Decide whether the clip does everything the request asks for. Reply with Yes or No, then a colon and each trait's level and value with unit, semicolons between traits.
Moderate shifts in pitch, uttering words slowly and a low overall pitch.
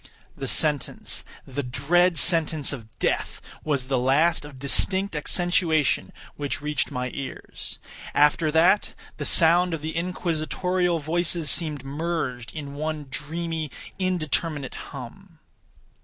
No: average, 3.2 semitones; slow, 110 wpm; medium, 155 Hz